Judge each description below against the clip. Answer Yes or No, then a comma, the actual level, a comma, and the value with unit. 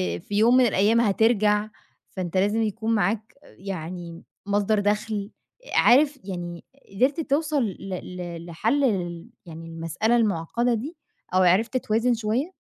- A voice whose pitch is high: Yes, high, 210 Hz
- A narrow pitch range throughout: No, average, 4.4 semitones